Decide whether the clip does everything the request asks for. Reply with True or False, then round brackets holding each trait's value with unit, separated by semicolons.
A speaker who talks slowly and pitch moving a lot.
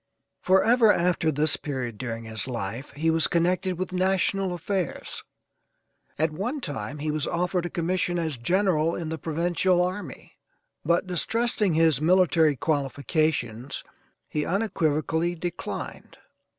False (125 wpm; 3.5 semitones)